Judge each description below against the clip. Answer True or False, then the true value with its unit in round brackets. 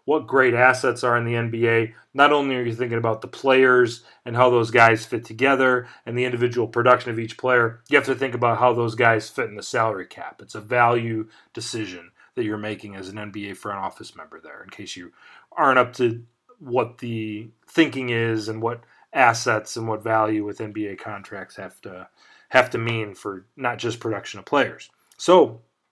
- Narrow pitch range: True (2.1 semitones)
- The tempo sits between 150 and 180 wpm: False (200 wpm)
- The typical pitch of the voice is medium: False (115 Hz)